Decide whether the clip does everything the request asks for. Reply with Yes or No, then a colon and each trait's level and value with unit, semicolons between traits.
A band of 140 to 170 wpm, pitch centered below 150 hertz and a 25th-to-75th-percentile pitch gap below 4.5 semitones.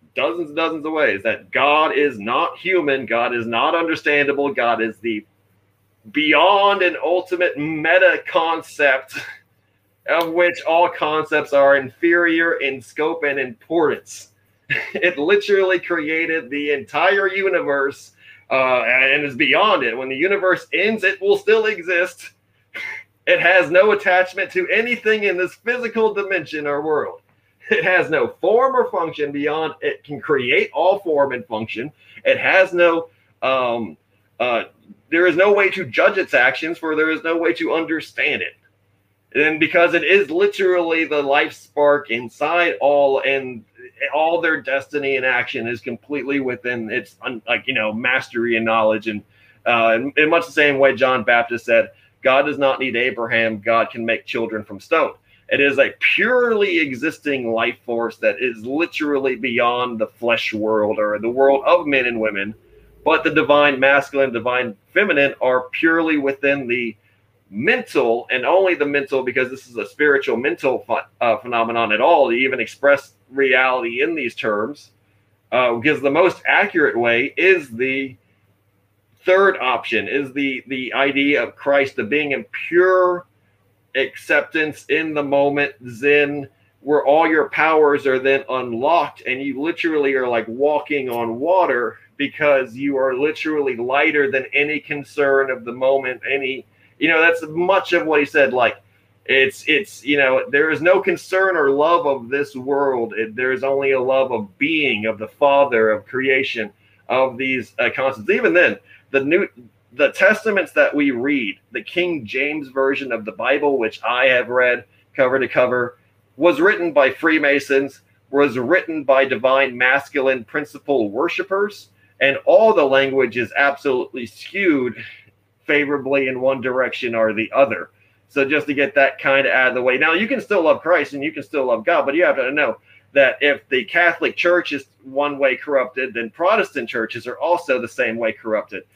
No: average, 165 wpm; medium, 140 Hz; average, 5.0 semitones